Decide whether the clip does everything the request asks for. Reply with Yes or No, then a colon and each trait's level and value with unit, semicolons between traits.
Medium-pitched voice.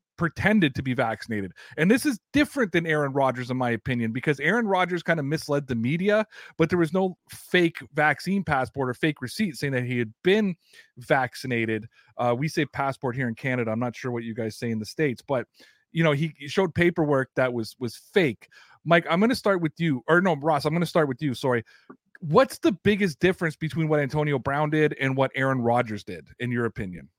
Yes: medium, 150 Hz